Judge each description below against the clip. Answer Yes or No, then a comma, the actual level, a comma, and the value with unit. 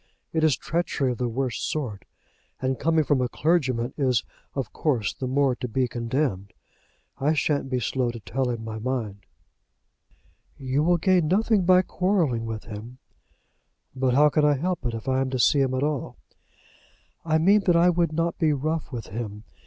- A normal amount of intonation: Yes, average, 4.7 semitones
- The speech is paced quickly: No, average, 185 wpm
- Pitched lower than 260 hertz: Yes, low, 135 Hz